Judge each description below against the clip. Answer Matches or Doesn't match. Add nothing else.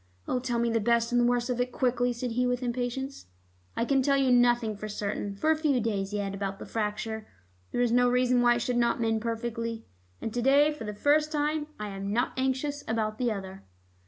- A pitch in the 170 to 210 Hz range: Doesn't match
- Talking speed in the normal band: Doesn't match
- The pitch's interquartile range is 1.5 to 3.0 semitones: Matches